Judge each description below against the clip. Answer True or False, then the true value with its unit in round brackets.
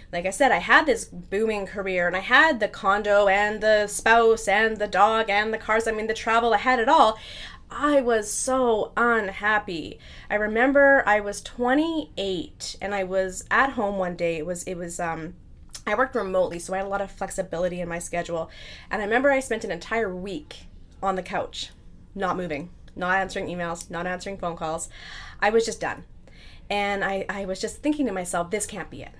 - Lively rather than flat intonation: False (3.3 semitones)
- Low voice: False (205 Hz)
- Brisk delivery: True (210 wpm)